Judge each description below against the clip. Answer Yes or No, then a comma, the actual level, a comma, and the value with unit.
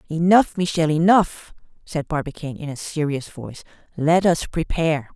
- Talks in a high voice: No, medium, 160 Hz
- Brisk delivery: No, average, 140 wpm